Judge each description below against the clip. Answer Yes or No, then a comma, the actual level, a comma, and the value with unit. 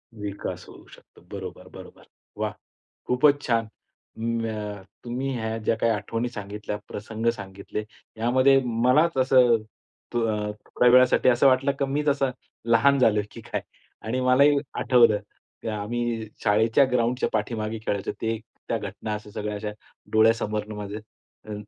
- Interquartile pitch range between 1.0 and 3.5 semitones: Yes, average, 3.1 semitones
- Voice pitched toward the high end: No, low, 115 Hz